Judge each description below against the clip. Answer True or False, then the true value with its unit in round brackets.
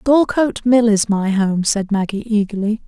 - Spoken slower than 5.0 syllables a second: True (4.7 syllables/s)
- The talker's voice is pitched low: False (215 Hz)